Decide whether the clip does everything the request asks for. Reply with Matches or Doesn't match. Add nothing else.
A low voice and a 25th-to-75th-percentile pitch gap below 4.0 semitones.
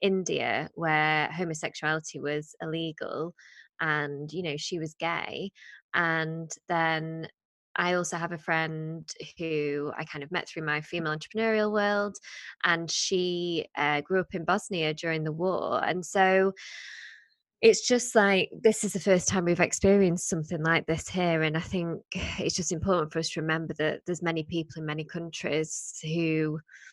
Doesn't match